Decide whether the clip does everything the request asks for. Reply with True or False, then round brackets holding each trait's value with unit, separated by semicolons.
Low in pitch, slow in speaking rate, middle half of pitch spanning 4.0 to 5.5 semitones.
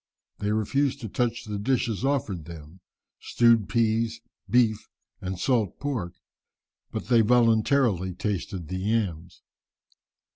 True (110 Hz; 115 wpm; 4.5 semitones)